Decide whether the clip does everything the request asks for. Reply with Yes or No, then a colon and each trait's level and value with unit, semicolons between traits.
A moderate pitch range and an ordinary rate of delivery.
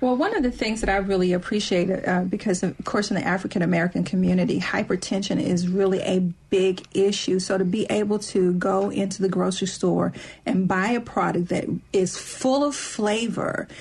No: narrow, 2.2 semitones; average, 185 wpm